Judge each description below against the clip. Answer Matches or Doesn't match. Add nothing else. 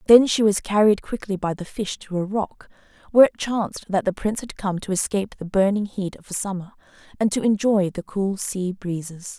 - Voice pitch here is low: Doesn't match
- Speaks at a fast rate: Matches